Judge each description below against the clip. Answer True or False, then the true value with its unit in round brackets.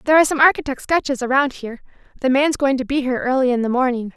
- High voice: True (265 Hz)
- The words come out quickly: True (245 wpm)